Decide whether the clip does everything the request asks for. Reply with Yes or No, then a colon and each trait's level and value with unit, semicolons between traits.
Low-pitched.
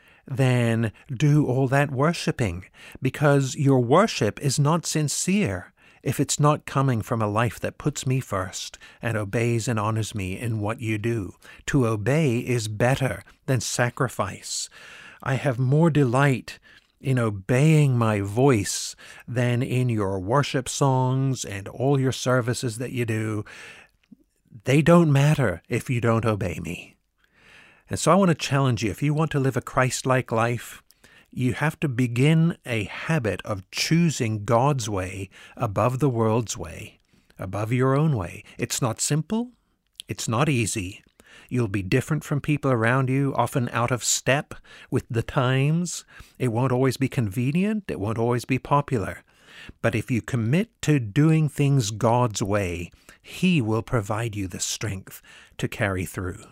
Yes: low, 125 Hz